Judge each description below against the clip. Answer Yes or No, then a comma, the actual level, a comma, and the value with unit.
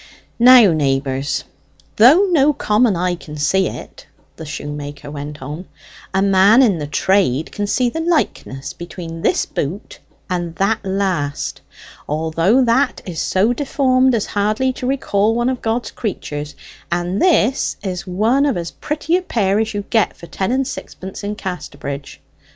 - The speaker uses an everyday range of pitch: No, wide, 6.9 semitones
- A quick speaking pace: No, average, 155 wpm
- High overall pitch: Yes, high, 195 Hz